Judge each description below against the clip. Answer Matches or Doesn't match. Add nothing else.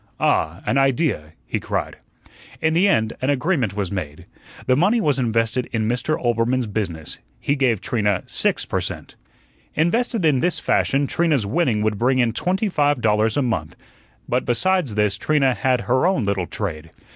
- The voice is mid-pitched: Doesn't match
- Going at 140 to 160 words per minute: Doesn't match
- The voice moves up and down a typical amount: Doesn't match